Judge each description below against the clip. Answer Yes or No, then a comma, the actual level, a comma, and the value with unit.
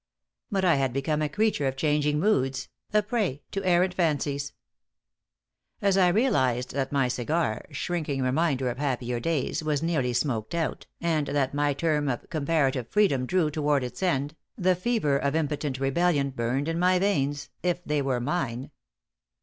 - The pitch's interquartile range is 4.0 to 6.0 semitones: Yes, average, 4.3 semitones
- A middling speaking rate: Yes, average, 165 wpm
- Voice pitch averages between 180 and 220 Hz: No, medium, 145 Hz